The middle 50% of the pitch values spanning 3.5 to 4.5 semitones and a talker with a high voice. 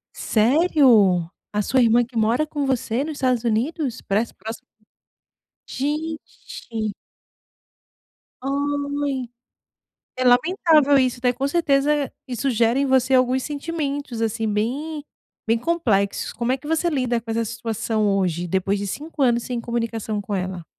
Yes: average, 4.2 semitones; high, 245 Hz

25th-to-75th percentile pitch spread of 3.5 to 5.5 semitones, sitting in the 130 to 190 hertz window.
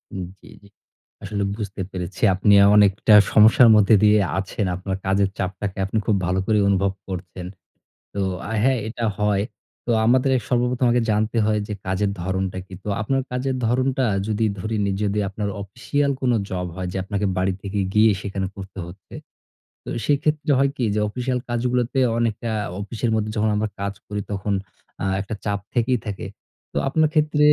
No: average, 3.8 semitones; low, 105 Hz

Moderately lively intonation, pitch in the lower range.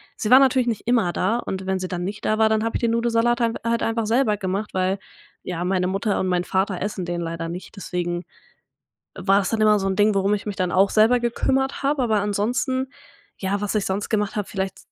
No: average, 3.4 semitones; high, 205 Hz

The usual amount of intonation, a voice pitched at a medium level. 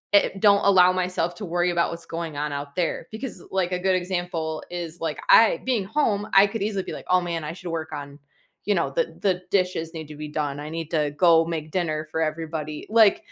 Yes: average, 3.1 semitones; medium, 170 Hz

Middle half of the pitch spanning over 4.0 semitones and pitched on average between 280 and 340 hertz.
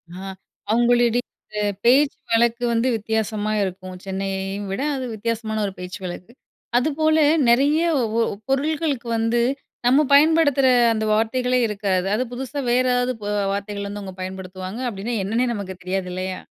No: average, 4.4 semitones; high, 225 Hz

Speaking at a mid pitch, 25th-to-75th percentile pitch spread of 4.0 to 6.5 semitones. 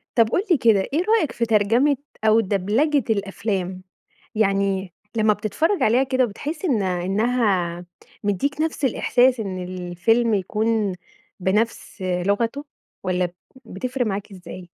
No: high, 215 Hz; average, 4.5 semitones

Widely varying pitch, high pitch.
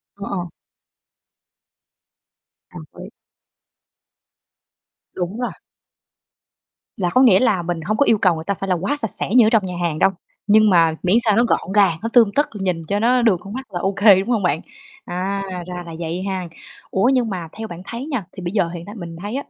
No: average, 3.9 semitones; high, 195 Hz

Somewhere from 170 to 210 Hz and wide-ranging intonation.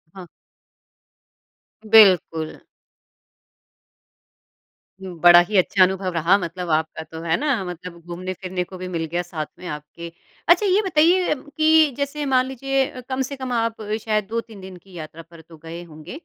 Yes: medium, 185 Hz; wide, 7.3 semitones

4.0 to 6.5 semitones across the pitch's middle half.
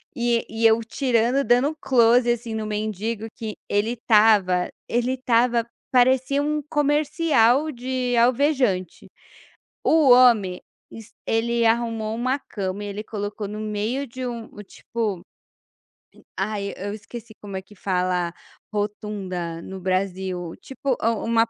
No: average, 3.4 semitones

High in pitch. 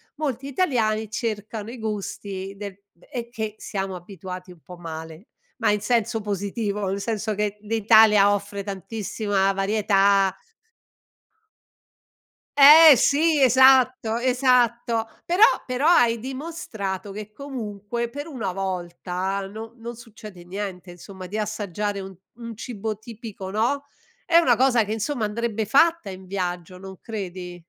Yes: high, 215 Hz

